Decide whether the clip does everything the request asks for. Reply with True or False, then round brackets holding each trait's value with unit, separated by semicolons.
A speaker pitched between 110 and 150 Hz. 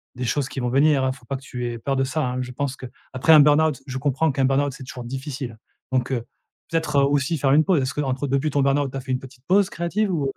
True (135 Hz)